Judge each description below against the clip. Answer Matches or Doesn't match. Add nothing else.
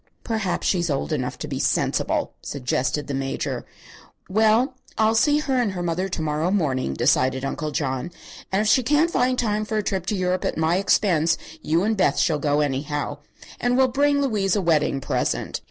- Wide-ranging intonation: Matches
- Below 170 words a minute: Doesn't match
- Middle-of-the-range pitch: Matches